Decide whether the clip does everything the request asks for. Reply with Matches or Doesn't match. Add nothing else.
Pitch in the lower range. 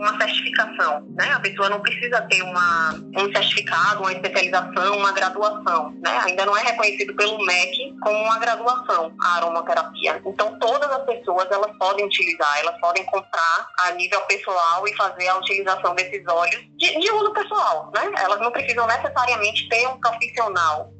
Doesn't match